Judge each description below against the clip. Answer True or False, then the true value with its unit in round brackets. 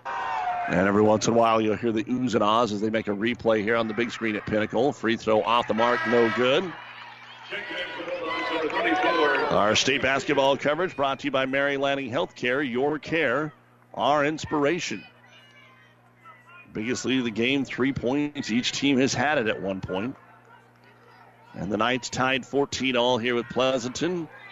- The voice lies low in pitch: True (125 Hz)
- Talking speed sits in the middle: True (170 wpm)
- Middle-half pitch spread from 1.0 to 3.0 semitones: False (3.5 semitones)